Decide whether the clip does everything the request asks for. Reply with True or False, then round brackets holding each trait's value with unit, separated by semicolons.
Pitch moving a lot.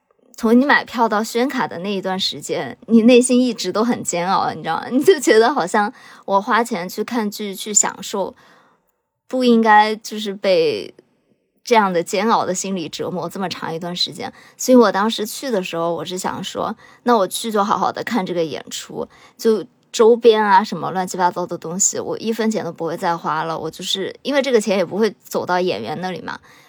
False (4.6 semitones)